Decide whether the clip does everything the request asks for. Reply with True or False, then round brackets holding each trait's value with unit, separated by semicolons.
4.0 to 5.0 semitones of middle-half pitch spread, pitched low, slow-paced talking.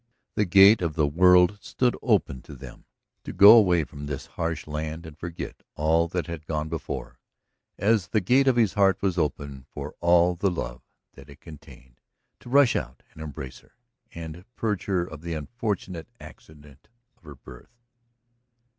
False (4.4 semitones; 85 Hz; 170 wpm)